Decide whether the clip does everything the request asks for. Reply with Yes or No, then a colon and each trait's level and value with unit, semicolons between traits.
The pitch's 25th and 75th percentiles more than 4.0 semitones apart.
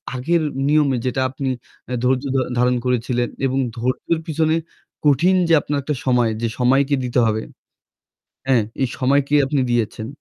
No: average, 2.7 semitones